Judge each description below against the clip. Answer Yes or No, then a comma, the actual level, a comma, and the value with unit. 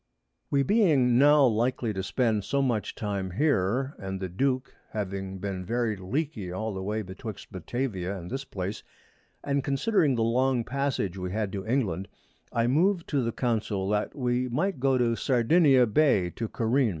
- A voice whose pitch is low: Yes, low, 115 Hz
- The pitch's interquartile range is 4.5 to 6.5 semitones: Yes, wide, 5.5 semitones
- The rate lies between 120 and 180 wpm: Yes, average, 170 wpm